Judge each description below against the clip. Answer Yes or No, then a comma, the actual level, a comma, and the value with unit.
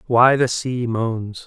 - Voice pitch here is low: Yes, low, 120 Hz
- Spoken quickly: No, average, 165 wpm